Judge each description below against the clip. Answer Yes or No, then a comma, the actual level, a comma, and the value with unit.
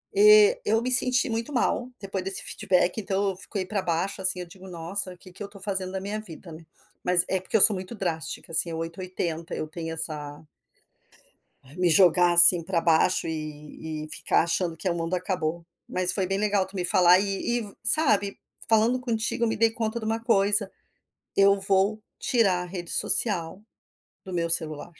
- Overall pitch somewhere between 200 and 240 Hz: No, high, 190 Hz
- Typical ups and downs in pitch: Yes, average, 3.7 semitones